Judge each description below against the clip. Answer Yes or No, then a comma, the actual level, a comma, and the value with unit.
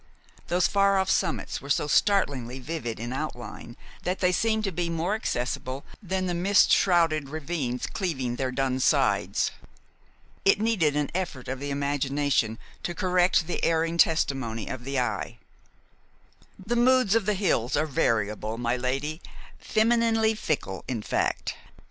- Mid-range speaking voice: Yes, medium, 155 Hz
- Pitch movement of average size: No, wide, 6.6 semitones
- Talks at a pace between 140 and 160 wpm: Yes, average, 150 wpm